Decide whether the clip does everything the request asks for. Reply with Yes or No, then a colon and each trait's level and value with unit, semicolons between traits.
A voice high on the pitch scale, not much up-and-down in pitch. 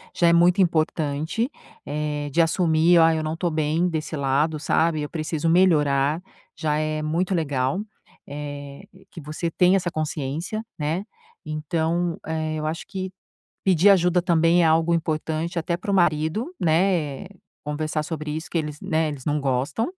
No: medium, 160 Hz; narrow, 2.2 semitones